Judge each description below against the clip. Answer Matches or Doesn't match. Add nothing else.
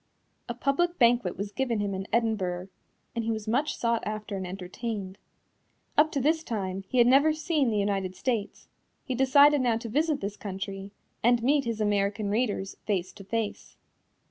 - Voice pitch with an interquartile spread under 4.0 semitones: Doesn't match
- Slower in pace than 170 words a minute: Doesn't match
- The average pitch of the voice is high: Matches